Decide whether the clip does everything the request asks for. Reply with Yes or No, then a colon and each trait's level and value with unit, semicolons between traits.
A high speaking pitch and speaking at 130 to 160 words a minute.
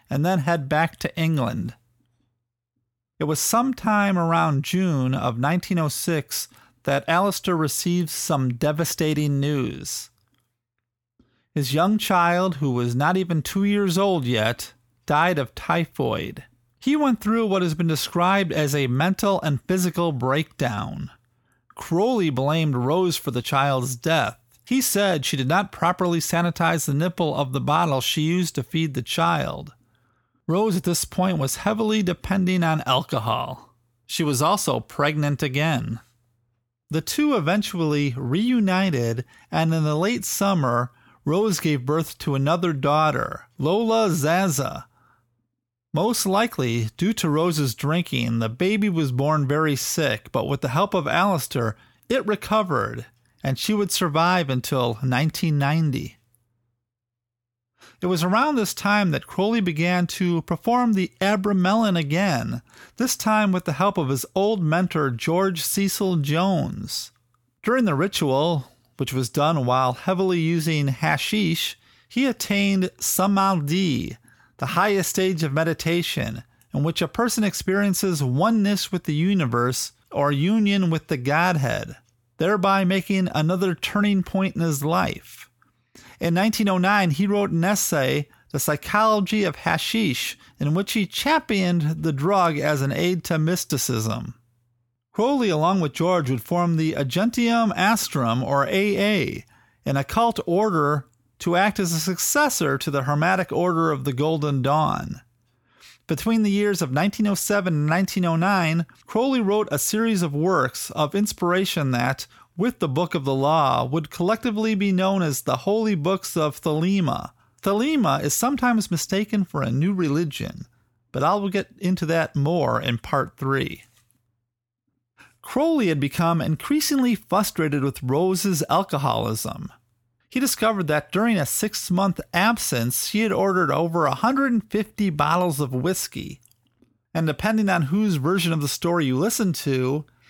No: medium, 165 Hz; average, 140 wpm